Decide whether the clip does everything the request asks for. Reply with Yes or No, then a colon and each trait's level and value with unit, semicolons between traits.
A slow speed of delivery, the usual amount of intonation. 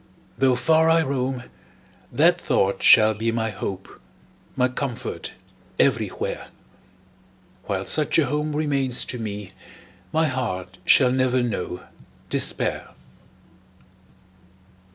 Yes: slow, 105 wpm; average, 4.5 semitones